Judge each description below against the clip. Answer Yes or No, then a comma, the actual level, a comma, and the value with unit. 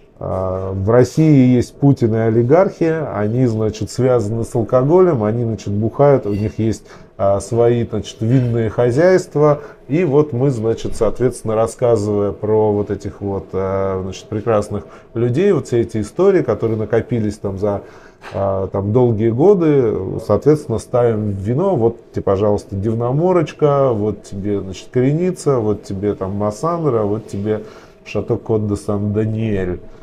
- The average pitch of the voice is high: No, low, 110 Hz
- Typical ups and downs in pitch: Yes, average, 3.7 semitones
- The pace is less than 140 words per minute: Yes, average, 130 wpm